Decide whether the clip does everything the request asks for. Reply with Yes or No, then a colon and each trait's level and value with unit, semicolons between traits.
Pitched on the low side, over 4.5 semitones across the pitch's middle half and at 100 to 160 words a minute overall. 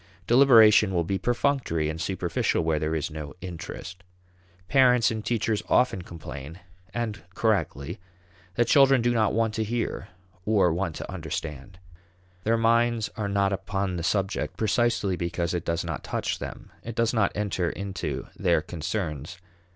Yes: low, 100 Hz; average, 5.1 semitones; average, 150 wpm